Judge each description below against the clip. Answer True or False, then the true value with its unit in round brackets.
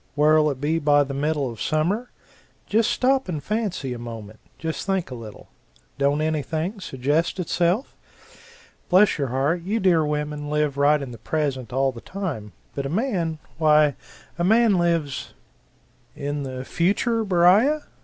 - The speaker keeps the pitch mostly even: False (4.7 semitones)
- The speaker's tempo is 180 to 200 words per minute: False (155 wpm)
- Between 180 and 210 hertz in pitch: False (155 Hz)